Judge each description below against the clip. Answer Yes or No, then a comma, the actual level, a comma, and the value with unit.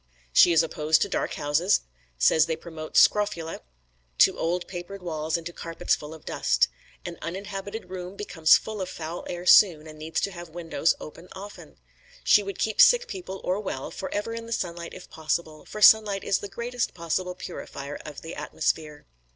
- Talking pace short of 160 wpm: No, average, 185 wpm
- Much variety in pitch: No, average, 3.8 semitones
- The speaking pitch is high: No, medium, 175 Hz